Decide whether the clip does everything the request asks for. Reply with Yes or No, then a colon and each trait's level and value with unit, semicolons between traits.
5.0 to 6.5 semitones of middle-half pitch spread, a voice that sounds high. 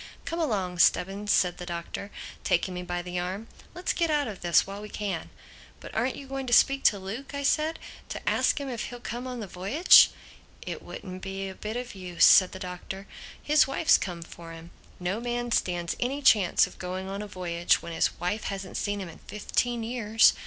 Yes: average, 5.3 semitones; high, 200 Hz